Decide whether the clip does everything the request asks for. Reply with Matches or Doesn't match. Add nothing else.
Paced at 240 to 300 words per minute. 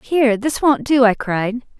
Doesn't match